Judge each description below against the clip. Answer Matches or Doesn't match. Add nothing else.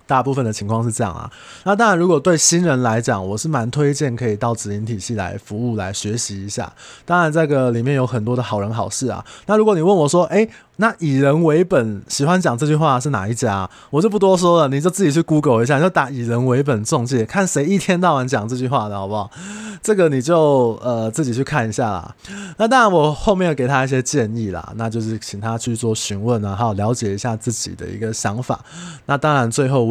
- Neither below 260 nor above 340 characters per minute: Doesn't match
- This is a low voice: Matches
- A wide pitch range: Matches